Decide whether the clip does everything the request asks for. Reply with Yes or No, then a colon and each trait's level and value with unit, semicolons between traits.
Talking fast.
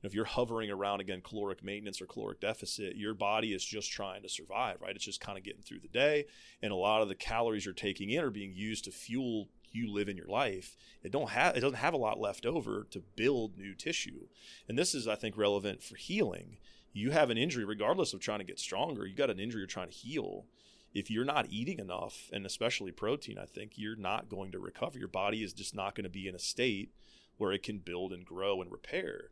Yes: fast, 245 wpm